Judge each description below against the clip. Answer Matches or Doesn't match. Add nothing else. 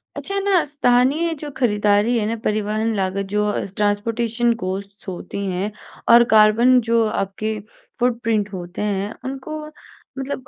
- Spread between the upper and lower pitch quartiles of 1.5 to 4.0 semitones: Matches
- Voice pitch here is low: Doesn't match